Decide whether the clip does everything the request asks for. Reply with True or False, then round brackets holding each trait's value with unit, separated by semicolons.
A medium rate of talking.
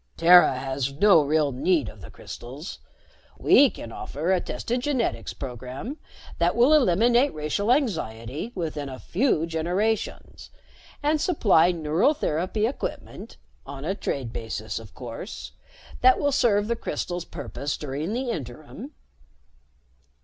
False (130 wpm)